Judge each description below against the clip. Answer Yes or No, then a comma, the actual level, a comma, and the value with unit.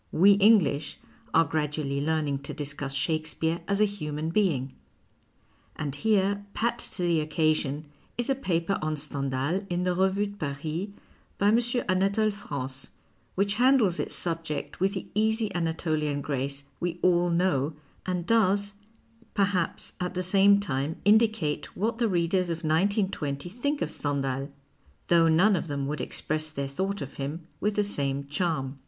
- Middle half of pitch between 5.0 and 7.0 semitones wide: Yes, average, 5.3 semitones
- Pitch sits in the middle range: Yes, medium, 170 Hz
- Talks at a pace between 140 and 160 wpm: Yes, average, 155 wpm